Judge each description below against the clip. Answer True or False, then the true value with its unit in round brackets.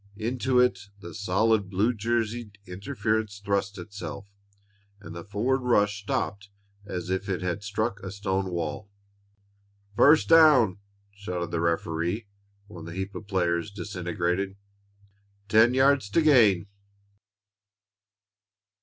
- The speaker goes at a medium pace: False (120 wpm)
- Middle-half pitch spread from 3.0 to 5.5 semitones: True (3.3 semitones)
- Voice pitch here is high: False (100 Hz)